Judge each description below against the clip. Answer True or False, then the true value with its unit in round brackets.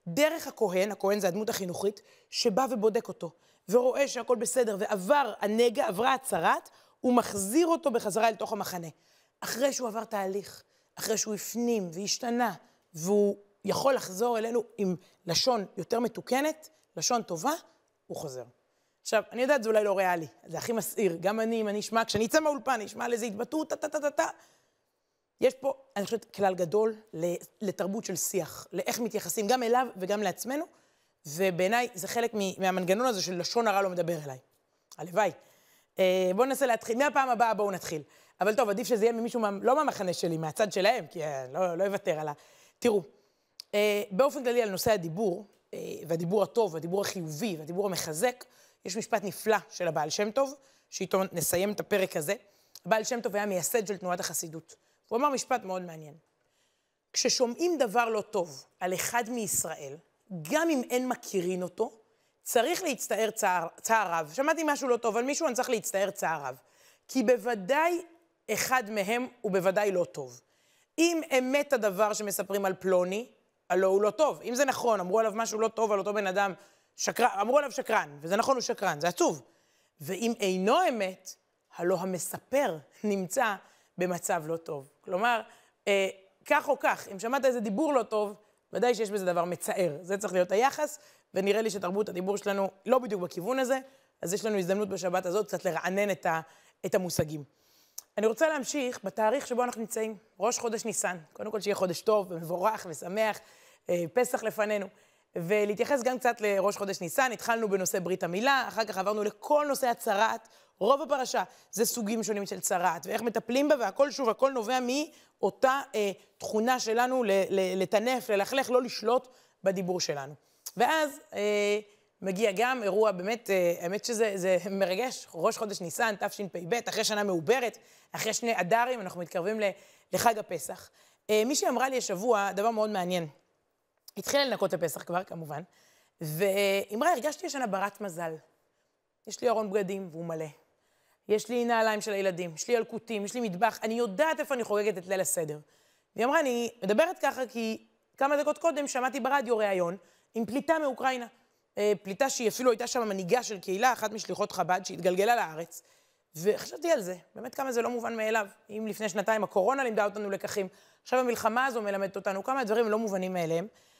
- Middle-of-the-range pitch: False (215 Hz)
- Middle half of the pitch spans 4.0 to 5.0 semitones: True (4.5 semitones)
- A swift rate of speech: True (165 wpm)